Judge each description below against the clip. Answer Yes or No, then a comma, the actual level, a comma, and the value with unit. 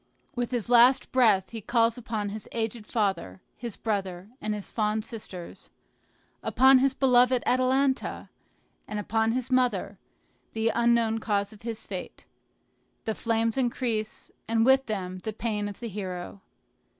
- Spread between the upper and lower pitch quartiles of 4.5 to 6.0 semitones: No, average, 2.7 semitones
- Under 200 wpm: Yes, average, 145 wpm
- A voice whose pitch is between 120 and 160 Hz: No, high, 225 Hz